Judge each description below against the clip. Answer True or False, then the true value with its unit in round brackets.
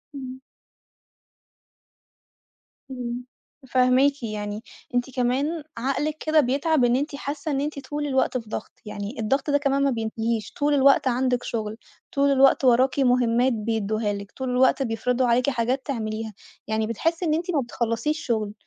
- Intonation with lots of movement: False (3.5 semitones)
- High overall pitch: True (255 Hz)